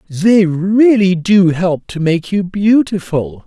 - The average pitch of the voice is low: No, medium, 185 Hz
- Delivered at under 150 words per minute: Yes, average, 140 wpm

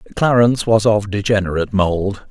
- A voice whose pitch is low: Yes, low, 105 Hz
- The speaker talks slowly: Yes, slow, 130 wpm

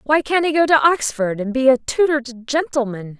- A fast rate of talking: Yes, fast, 225 wpm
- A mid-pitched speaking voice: No, very high, 270 Hz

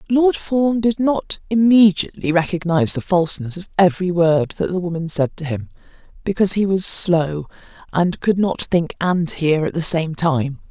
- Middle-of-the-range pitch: Yes, medium, 180 Hz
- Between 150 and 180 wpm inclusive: Yes, average, 175 wpm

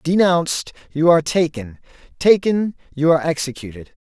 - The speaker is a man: Yes, male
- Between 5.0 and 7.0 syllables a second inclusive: Yes, 5.4 syllables/s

